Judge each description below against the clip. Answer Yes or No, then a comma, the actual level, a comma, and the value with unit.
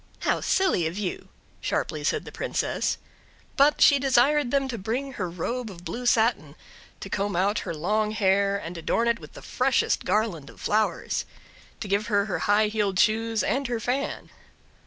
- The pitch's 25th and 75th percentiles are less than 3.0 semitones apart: No, average, 3.9 semitones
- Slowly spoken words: No, average, 180 wpm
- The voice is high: Yes, high, 215 Hz